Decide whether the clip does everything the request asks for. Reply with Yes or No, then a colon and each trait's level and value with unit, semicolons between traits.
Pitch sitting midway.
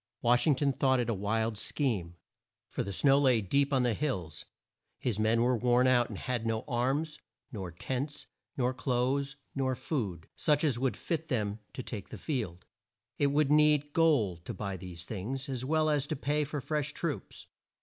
No: low, 130 Hz